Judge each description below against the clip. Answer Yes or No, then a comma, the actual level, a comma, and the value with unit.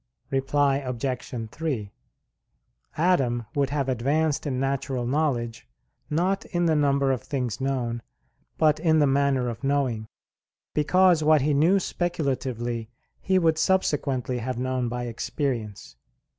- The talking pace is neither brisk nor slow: No, slow, 130 wpm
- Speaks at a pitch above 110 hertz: Yes, low, 135 Hz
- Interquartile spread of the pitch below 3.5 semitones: No, average, 3.8 semitones